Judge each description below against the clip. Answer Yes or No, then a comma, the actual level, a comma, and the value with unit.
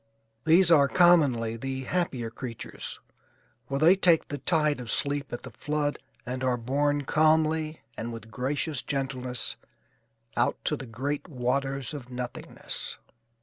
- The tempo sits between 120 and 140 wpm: Yes, slow, 135 wpm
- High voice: No, medium, 140 Hz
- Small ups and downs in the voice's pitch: No, average, 3.5 semitones